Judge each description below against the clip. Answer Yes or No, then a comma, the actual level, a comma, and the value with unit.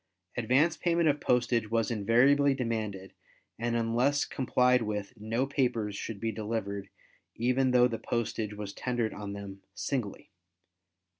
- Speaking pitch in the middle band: No, low, 115 Hz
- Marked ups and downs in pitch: No, average, 3.1 semitones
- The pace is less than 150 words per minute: Yes, slow, 135 wpm